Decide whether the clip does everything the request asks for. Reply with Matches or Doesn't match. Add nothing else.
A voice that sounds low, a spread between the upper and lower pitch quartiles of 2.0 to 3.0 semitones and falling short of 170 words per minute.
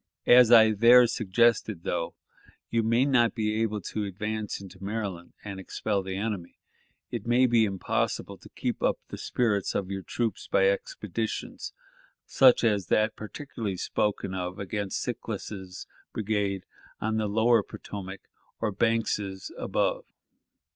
Matches